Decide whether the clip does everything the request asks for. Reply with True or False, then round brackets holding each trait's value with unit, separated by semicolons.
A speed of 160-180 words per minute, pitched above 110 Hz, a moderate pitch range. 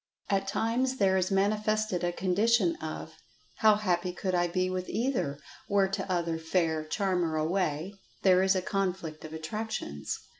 False (145 wpm; 185 Hz; 3.1 semitones)